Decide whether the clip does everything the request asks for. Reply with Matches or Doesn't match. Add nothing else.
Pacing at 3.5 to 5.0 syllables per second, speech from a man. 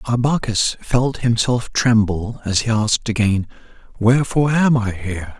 Matches